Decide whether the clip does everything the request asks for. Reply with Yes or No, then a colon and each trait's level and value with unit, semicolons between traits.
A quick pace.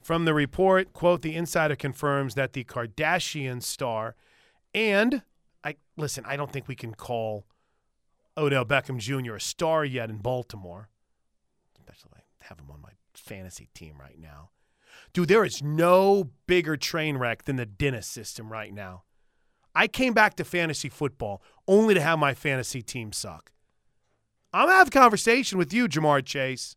No: average, 165 wpm